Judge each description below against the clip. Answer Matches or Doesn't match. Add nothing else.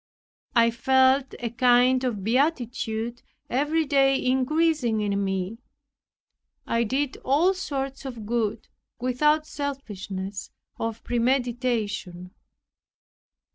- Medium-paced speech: Doesn't match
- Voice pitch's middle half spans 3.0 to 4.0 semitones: Matches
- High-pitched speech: Matches